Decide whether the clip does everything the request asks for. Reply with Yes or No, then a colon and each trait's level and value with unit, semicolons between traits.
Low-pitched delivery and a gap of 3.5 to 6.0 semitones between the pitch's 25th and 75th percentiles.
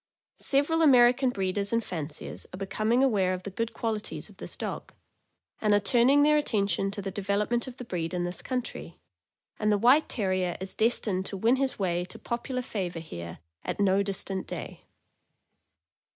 No: high, 205 Hz; average, 4.4 semitones